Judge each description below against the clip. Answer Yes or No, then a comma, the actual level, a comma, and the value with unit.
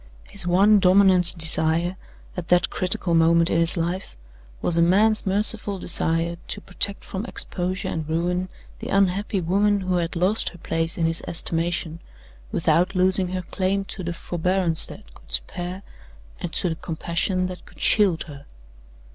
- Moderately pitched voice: Yes, medium, 180 Hz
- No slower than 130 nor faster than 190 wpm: Yes, average, 160 wpm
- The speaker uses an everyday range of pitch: No, narrow, 2.2 semitones